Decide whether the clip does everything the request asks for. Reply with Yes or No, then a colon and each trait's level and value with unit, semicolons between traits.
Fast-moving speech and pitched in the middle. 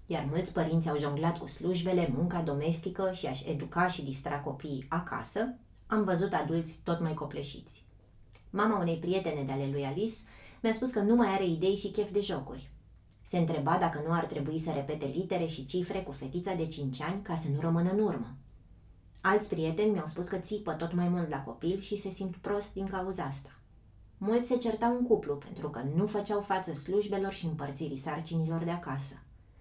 Yes: fast, 195 wpm; medium, 165 Hz